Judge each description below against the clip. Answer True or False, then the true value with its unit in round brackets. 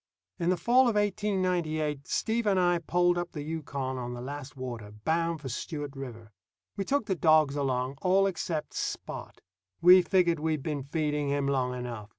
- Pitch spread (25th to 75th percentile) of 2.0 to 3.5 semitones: False (4.7 semitones)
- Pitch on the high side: False (155 Hz)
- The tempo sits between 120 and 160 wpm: False (175 wpm)